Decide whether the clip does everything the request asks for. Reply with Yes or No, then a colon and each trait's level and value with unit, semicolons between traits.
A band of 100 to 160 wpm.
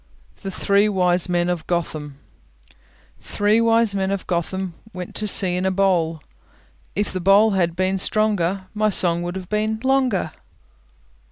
Yes: average, 155 wpm